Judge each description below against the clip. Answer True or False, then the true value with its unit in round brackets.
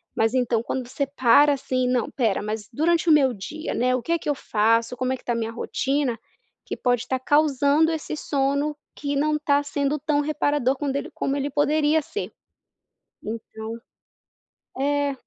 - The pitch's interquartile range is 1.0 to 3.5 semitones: True (3.1 semitones)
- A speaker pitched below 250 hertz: False (275 Hz)